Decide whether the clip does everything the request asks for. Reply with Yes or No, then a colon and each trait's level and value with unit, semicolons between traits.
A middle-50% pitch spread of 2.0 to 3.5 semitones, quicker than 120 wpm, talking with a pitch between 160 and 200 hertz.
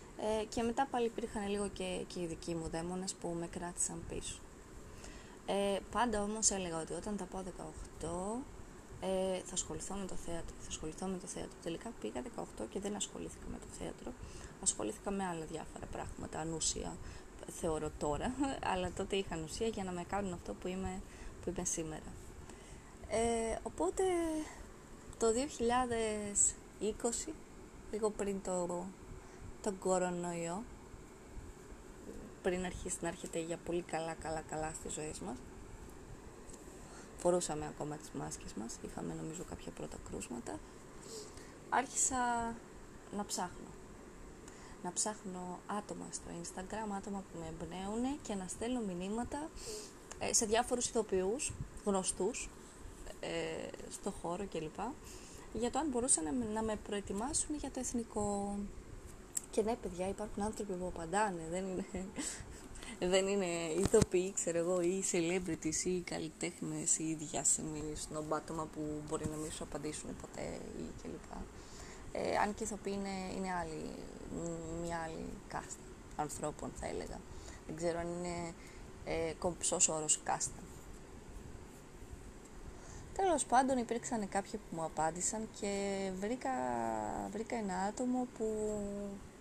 No: average, 4.5 semitones; average, 130 wpm; high, 190 Hz